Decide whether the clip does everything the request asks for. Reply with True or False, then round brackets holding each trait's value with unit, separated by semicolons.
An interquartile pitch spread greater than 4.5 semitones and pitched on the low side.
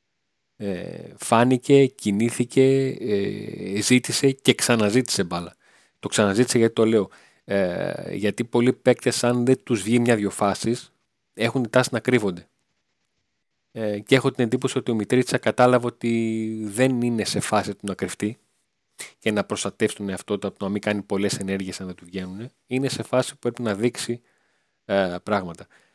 False (3.5 semitones; 115 Hz)